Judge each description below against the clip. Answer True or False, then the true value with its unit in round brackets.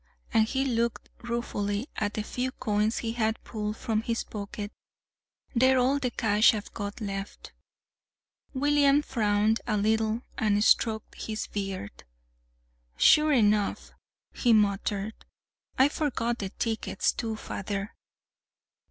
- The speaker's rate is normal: False (125 wpm)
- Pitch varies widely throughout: False (2.6 semitones)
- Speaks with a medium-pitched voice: False (220 Hz)